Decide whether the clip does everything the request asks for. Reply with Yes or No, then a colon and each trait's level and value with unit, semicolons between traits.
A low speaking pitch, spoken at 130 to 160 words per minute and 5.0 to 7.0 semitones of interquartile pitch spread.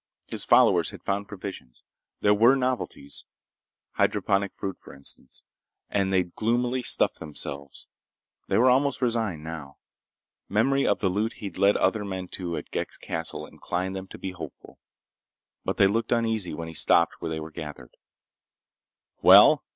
Yes: very low, 95 Hz; average, 150 wpm; wide, 5.4 semitones